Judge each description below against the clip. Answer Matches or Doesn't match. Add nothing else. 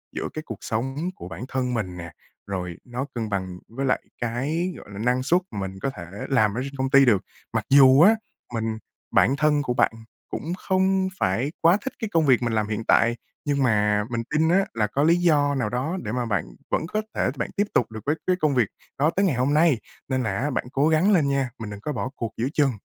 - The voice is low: Matches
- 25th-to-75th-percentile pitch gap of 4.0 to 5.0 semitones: Doesn't match